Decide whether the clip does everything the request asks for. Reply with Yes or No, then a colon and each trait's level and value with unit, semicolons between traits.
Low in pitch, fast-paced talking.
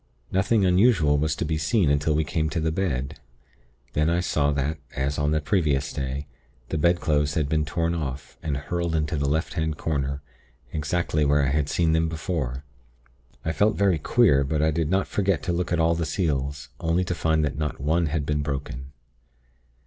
No: very low, 80 Hz; average, 195 wpm